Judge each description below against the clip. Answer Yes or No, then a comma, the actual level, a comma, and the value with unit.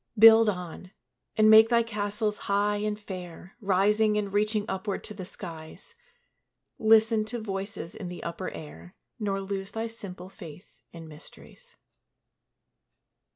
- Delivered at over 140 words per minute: No, slow, 135 wpm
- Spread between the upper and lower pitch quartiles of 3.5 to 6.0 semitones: No, average, 2.8 semitones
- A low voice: No, high, 205 Hz